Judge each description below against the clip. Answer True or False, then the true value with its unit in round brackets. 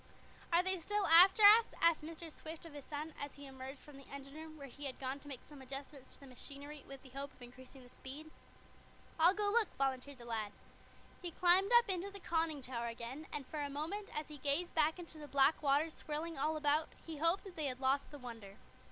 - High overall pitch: True (295 Hz)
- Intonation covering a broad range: False (3.5 semitones)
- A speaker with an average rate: False (230 wpm)